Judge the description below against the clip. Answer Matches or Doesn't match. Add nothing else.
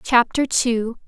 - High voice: Matches